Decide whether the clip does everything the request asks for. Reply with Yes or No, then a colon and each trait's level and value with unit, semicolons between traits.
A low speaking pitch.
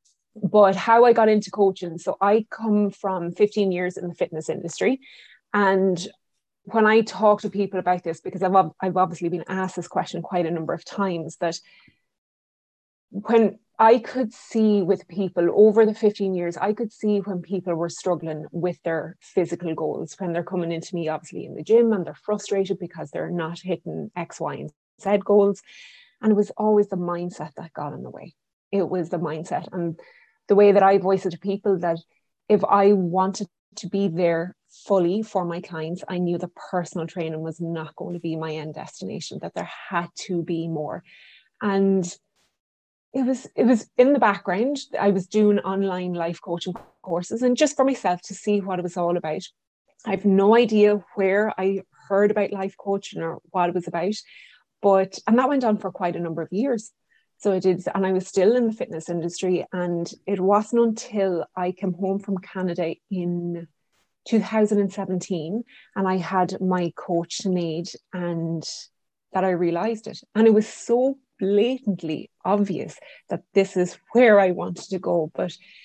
No: high, 190 Hz